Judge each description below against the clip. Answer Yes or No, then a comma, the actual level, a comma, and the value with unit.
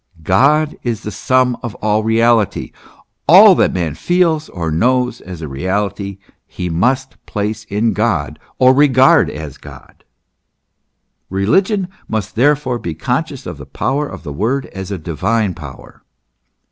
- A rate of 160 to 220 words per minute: No, average, 145 wpm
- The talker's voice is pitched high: No, low, 110 Hz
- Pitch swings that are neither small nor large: No, wide, 5.9 semitones